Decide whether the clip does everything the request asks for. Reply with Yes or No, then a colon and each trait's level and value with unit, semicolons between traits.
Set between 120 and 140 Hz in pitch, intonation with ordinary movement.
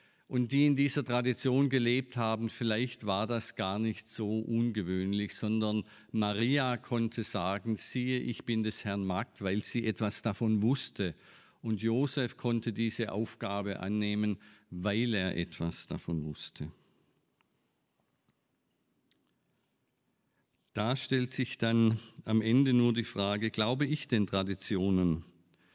No: low, 110 Hz; average, 3.0 semitones